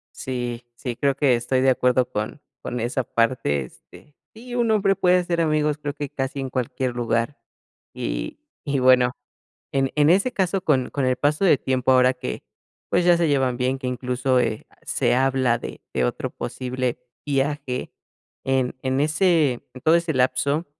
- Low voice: Yes, low, 130 Hz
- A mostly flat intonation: No, average, 3.1 semitones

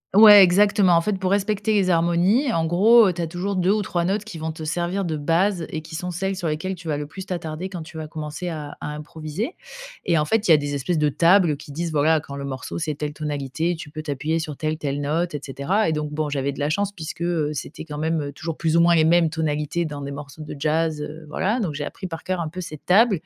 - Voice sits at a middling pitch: Yes, medium, 165 Hz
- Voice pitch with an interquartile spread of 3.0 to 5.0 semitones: Yes, average, 3.4 semitones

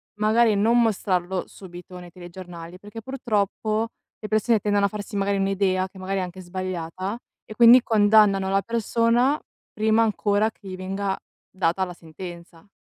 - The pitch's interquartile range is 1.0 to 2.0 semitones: No, average, 2.7 semitones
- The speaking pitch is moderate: No, high, 200 Hz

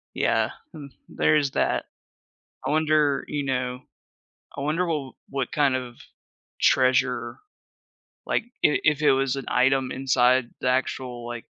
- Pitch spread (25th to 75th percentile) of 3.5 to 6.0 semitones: No, narrow, 2.5 semitones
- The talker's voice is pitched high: No, low, 135 Hz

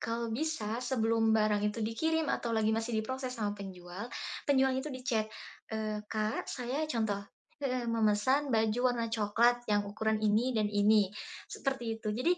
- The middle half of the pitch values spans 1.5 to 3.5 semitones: Yes, average, 2.8 semitones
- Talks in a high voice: Yes, high, 225 Hz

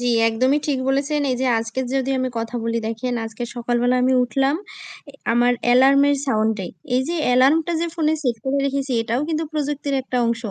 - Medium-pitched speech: No, very high, 260 Hz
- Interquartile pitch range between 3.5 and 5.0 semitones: No, average, 2.7 semitones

